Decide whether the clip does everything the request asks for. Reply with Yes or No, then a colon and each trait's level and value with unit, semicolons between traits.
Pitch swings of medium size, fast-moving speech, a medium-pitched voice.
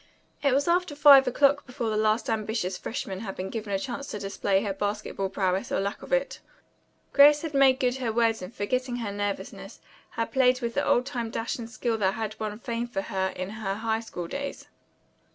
No: average, 4.1 semitones; fast, 210 wpm; high, 225 Hz